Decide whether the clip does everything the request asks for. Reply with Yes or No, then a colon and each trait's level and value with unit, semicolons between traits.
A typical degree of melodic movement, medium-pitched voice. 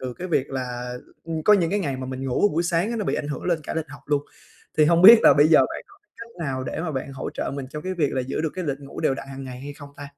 Yes: average, 4.2 semitones; medium, 145 Hz